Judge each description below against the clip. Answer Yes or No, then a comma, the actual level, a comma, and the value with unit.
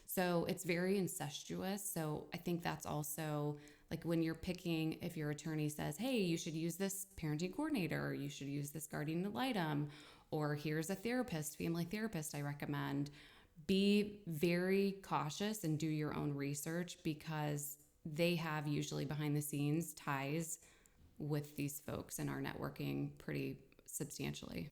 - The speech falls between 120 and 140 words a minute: No, average, 155 wpm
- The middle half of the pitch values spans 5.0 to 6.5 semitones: No, average, 3.0 semitones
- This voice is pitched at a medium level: Yes, medium, 155 Hz